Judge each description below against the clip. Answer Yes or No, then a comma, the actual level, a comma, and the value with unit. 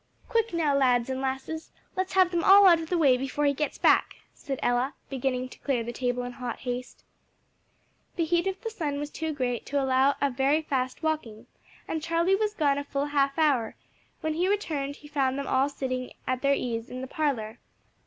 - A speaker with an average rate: No, fast, 210 wpm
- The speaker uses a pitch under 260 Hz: No, very high, 280 Hz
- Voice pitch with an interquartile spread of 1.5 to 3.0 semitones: No, average, 3.8 semitones